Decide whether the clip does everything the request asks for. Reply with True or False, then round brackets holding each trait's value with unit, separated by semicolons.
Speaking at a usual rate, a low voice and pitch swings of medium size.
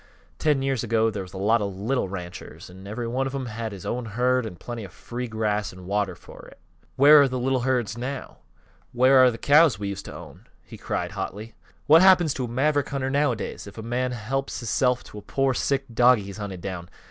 False (230 wpm; 120 Hz; 4.4 semitones)